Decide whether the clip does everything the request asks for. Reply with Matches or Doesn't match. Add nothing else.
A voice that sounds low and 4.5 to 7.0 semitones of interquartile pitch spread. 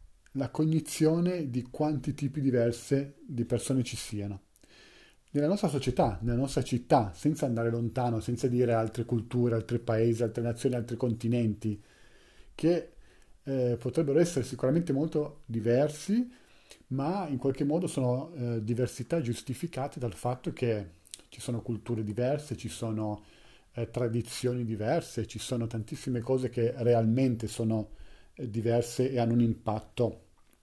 Doesn't match